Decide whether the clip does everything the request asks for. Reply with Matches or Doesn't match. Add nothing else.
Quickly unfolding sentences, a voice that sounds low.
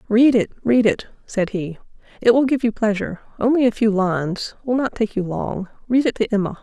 Doesn't match